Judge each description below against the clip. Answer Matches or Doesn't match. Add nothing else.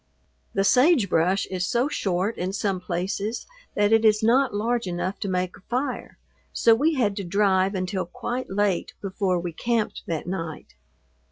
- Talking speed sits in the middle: Matches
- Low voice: Doesn't match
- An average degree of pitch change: Matches